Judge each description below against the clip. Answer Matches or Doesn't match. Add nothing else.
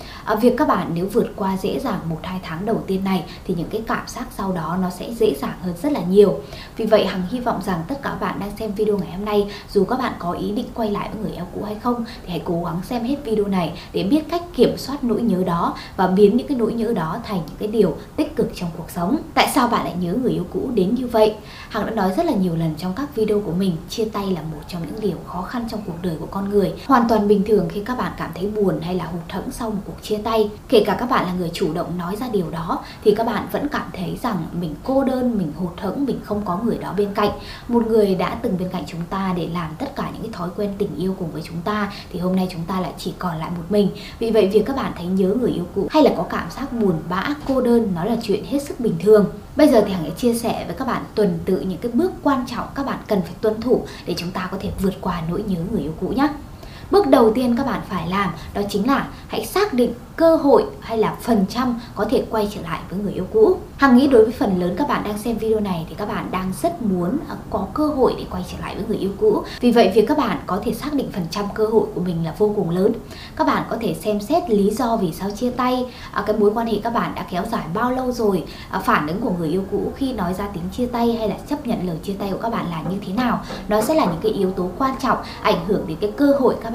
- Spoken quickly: Matches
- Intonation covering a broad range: Doesn't match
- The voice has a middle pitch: Doesn't match